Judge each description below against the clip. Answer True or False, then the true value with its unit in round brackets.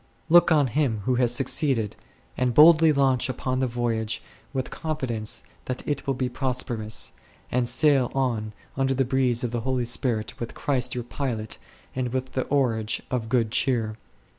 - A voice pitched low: True (125 Hz)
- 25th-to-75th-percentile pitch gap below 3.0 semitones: True (2.5 semitones)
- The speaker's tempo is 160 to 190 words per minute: True (175 wpm)